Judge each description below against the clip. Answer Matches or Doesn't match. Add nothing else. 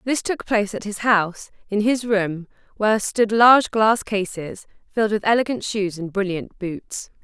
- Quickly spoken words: Doesn't match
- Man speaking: Doesn't match